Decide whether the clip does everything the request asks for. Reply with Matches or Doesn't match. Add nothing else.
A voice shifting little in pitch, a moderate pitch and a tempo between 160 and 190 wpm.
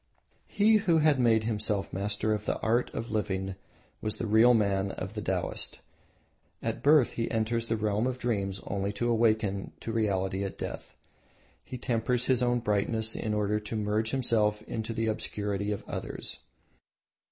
Doesn't match